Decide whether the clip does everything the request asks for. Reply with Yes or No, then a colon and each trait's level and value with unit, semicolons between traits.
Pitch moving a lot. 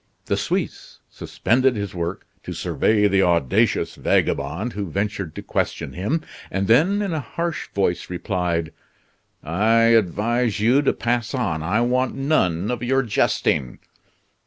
Yes: wide, 5.7 semitones